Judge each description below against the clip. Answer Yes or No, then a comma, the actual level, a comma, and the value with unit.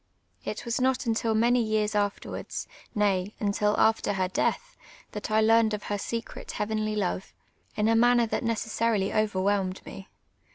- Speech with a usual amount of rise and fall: No, narrow, 2.0 semitones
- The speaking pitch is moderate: No, high, 215 Hz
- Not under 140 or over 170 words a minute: Yes, average, 155 wpm